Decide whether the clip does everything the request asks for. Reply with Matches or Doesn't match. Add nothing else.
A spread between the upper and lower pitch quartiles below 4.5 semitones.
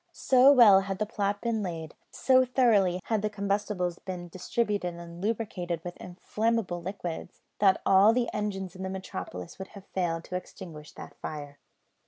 Matches